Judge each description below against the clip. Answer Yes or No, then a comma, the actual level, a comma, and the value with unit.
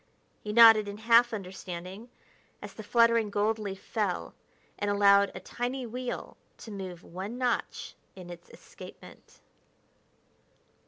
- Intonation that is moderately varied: Yes, average, 3.2 semitones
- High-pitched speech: Yes, high, 210 Hz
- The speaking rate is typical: No, slow, 125 wpm